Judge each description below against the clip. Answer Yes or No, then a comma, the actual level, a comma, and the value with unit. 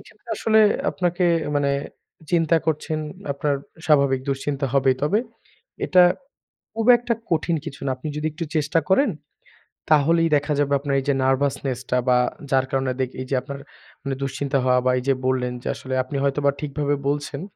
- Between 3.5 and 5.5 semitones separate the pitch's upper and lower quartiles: No, average, 3.0 semitones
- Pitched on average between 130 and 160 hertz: Yes, medium, 140 Hz